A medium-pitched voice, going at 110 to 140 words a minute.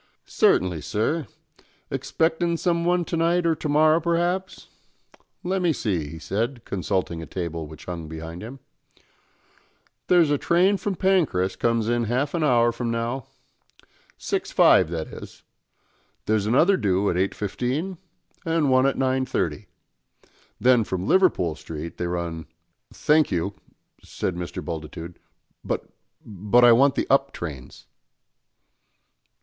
No: low, 120 Hz; slow, 135 wpm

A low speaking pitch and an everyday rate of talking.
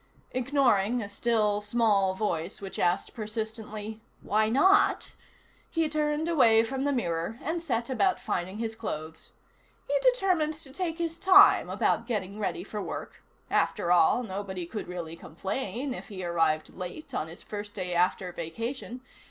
No: high, 220 Hz; average, 150 wpm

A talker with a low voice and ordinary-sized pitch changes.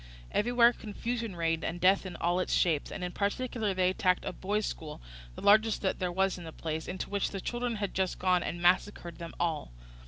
No: medium, 185 Hz; average, 3.1 semitones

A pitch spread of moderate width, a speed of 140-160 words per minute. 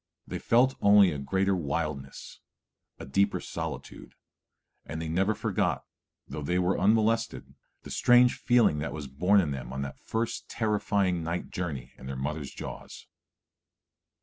No: wide, 6.4 semitones; average, 150 wpm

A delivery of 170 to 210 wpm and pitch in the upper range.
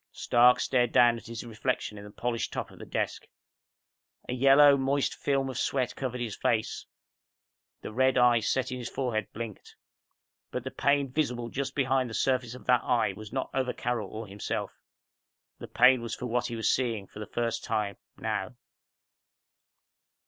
No: average, 180 wpm; low, 120 Hz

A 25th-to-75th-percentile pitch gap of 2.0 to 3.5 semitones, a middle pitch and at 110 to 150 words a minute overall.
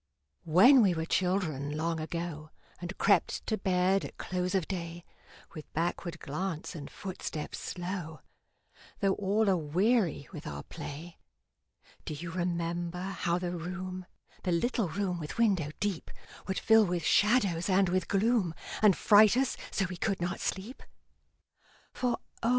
Yes: average, 2.8 semitones; medium, 180 Hz; average, 145 wpm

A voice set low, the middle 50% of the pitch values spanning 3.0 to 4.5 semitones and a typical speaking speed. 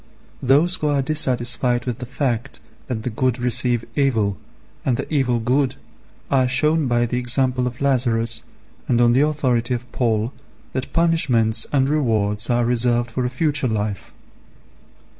No: low, 125 Hz; narrow, 2.4 semitones; average, 155 wpm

